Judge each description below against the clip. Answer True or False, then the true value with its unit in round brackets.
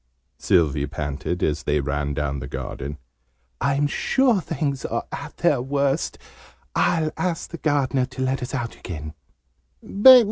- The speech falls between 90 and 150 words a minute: True (140 wpm)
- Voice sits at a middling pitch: False (125 Hz)